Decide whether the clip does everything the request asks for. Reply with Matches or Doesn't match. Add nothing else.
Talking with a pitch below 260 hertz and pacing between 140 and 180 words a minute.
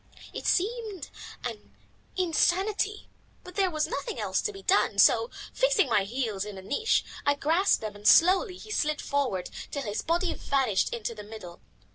Doesn't match